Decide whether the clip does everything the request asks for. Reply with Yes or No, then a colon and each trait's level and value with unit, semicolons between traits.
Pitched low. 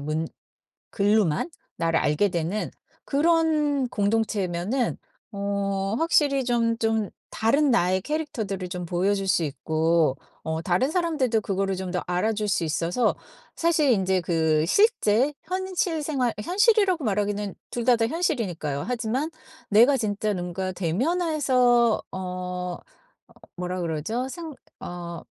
No: high, 210 Hz